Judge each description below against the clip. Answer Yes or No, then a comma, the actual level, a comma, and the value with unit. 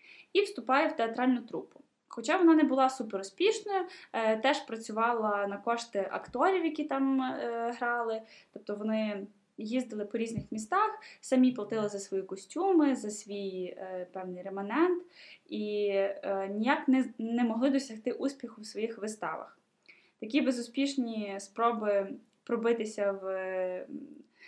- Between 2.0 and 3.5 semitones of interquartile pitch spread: No, average, 5.0 semitones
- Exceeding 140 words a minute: No, average, 130 wpm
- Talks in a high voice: Yes, high, 235 Hz